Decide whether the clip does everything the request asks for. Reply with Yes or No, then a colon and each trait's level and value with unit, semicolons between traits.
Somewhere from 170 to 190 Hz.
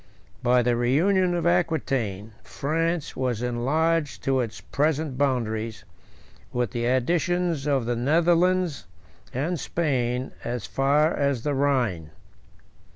No: low, 135 Hz